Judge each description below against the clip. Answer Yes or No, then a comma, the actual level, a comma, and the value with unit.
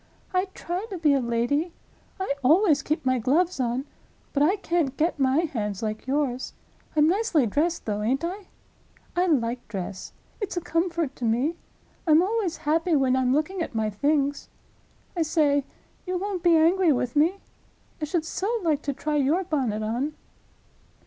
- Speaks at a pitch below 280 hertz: No, very high, 300 Hz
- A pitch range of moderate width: Yes, average, 5.0 semitones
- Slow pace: No, average, 160 wpm